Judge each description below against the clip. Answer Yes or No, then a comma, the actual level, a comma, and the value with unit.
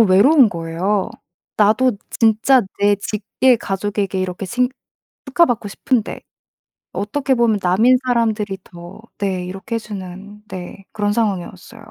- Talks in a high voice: Yes, high, 205 Hz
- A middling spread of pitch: Yes, average, 3.4 semitones